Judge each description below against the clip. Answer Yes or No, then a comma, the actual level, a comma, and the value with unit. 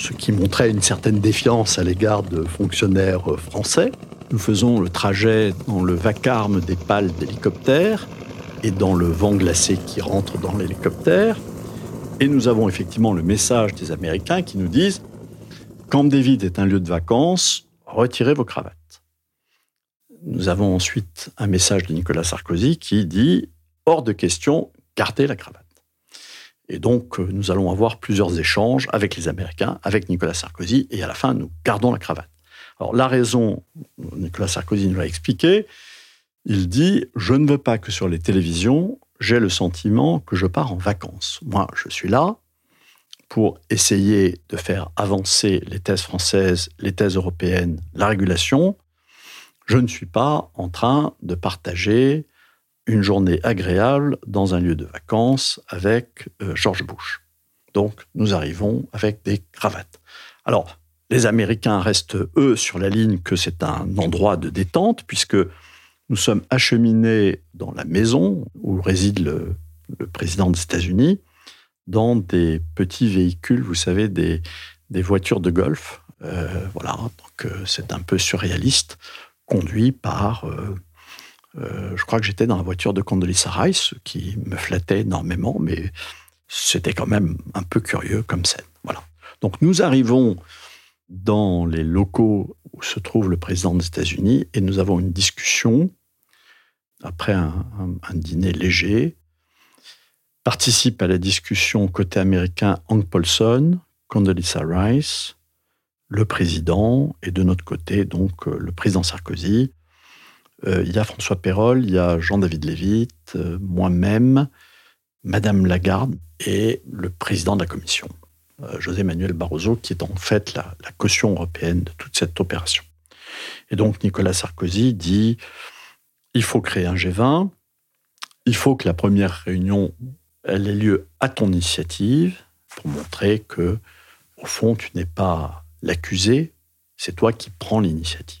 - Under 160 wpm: Yes, average, 150 wpm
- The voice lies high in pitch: No, very low, 95 Hz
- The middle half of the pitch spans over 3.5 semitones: Yes, average, 4.1 semitones